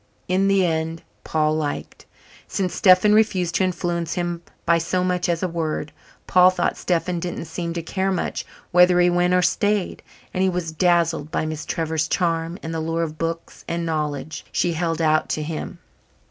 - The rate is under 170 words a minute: No, average, 185 wpm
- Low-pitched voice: No, medium, 170 Hz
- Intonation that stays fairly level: Yes, narrow, 1.9 semitones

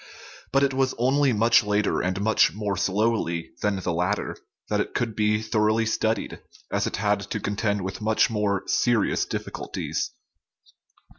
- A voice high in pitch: No, low, 105 Hz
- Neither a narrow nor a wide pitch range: No, narrow, 2.2 semitones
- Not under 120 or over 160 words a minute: Yes, average, 155 wpm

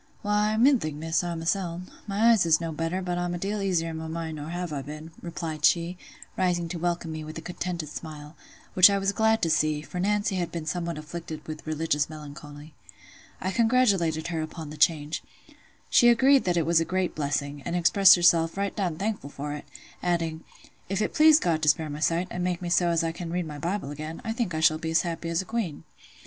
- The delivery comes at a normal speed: No, fast, 225 wpm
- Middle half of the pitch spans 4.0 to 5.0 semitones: No, average, 2.8 semitones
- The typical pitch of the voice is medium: Yes, medium, 170 Hz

